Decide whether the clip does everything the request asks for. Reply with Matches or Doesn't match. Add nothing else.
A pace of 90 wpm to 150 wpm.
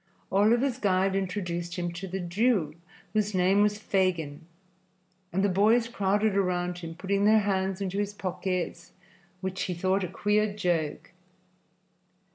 Matches